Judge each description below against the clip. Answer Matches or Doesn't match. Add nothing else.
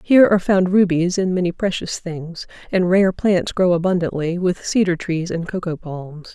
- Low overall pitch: Doesn't match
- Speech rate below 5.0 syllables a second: Matches